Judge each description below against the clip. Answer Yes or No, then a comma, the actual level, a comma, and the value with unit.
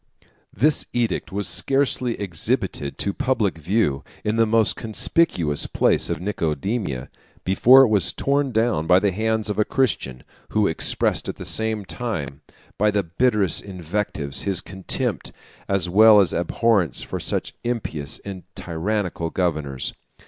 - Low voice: Yes, low, 100 Hz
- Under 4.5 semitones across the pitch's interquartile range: No, average, 5.1 semitones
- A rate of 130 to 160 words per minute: Yes, average, 150 wpm